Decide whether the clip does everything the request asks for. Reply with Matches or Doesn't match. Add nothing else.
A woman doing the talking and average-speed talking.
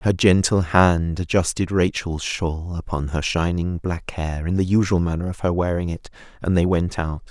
Doesn't match